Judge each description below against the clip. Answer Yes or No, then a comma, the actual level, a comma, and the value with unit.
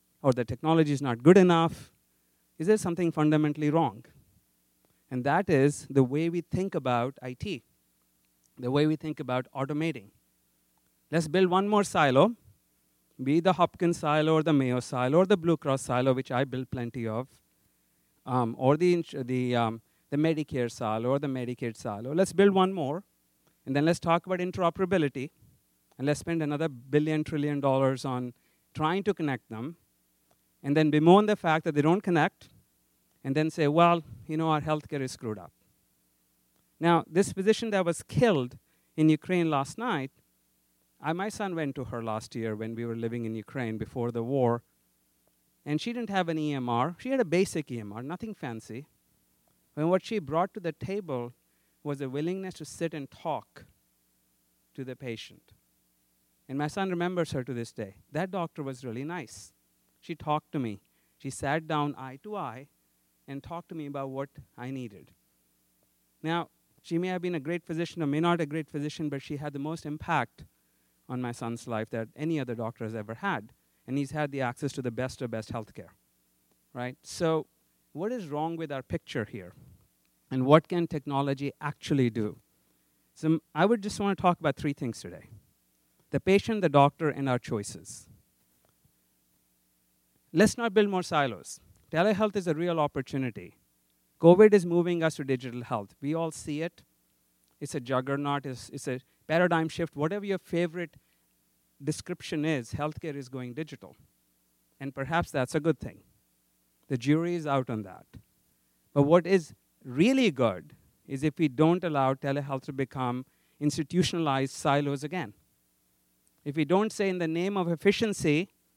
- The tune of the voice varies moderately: No, wide, 6.7 semitones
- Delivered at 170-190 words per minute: Yes, average, 175 wpm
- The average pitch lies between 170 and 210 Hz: No, medium, 140 Hz